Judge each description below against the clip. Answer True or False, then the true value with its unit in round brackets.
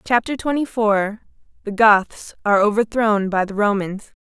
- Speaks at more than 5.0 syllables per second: False (4.6 syllables/s)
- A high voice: True (210 Hz)